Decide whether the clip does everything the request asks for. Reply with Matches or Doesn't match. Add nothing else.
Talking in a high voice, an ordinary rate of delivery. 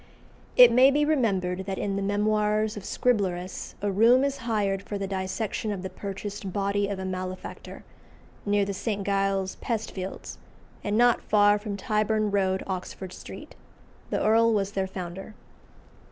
Matches